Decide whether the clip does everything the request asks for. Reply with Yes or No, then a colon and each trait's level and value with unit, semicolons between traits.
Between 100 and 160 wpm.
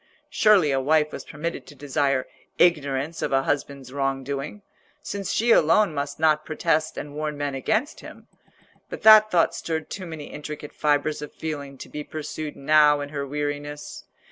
No: average, 170 wpm